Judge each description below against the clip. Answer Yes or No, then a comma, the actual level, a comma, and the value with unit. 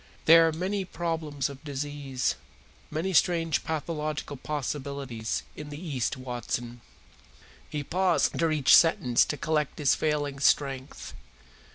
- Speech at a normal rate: No, slow, 125 wpm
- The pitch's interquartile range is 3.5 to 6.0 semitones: No, average, 2.9 semitones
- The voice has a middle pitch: Yes, medium, 150 Hz